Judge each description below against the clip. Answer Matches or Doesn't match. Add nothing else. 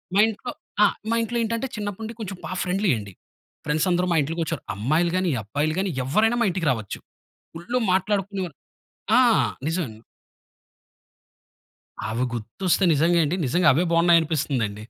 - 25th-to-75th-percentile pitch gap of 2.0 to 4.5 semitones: Doesn't match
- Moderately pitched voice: Matches